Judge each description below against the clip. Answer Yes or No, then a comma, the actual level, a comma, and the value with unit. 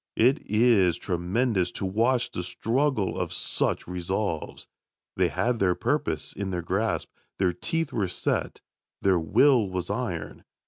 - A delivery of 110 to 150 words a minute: Yes, average, 140 wpm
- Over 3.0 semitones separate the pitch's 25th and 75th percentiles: Yes, average, 4.9 semitones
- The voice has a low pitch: Yes, low, 100 Hz